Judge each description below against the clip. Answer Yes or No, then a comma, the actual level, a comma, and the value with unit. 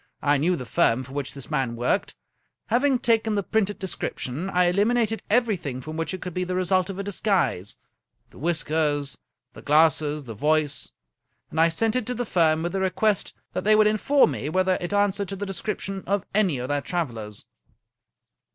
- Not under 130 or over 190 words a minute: No, fast, 205 wpm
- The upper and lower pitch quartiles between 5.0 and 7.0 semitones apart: Yes, wide, 5.6 semitones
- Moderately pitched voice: Yes, medium, 180 Hz